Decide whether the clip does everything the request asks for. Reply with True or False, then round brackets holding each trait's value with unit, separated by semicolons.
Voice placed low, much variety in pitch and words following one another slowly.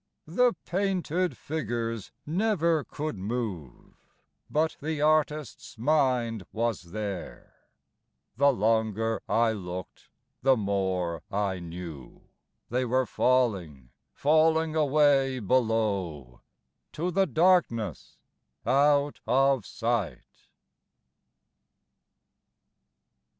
True (120 Hz; 7.1 semitones; 80 wpm)